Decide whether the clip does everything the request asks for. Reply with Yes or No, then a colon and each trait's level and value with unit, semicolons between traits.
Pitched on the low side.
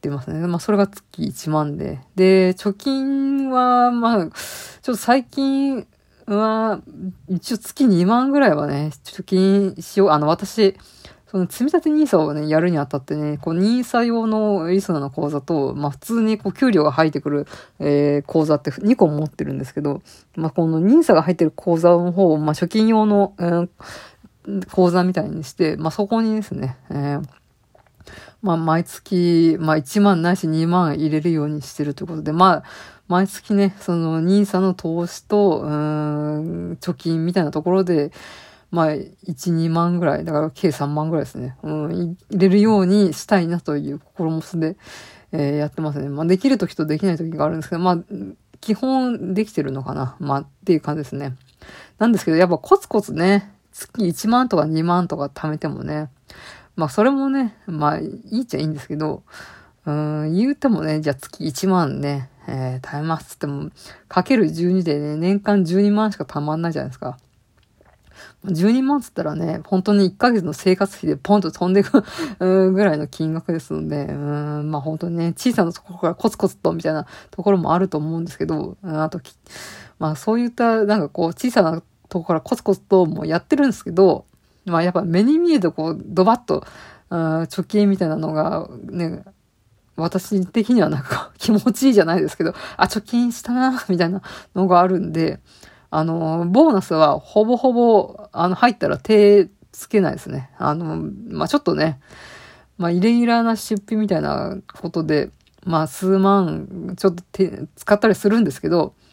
No: medium, 175 Hz